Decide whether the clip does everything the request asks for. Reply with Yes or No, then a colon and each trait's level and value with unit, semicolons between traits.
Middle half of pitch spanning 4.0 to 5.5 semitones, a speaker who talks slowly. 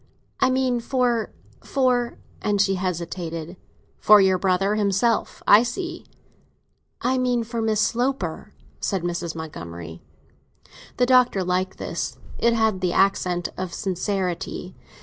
Yes: average, 5.0 semitones; slow, 120 wpm